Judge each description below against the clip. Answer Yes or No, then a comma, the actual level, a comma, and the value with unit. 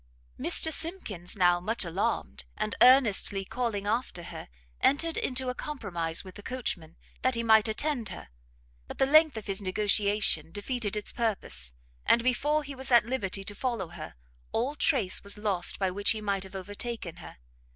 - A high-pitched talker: Yes, high, 210 Hz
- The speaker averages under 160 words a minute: No, average, 170 wpm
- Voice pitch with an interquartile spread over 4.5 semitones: Yes, average, 5.0 semitones